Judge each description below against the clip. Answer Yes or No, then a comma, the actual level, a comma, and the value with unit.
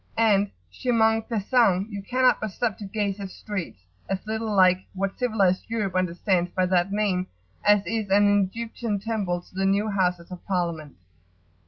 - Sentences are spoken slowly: No, average, 165 wpm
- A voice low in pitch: No, high, 200 Hz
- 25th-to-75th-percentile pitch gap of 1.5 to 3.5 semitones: Yes, average, 3.0 semitones